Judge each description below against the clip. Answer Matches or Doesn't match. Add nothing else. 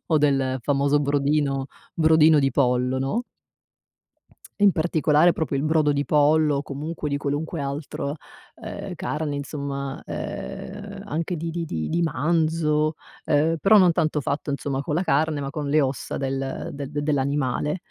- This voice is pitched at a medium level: Matches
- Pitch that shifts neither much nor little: Doesn't match